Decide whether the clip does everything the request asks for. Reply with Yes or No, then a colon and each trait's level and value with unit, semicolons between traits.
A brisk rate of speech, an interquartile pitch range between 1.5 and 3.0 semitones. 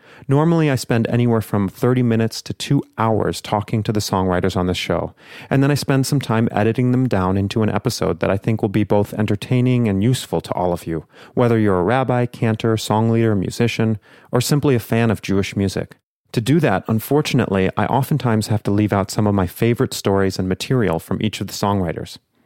No: fast, 210 wpm; average, 4.0 semitones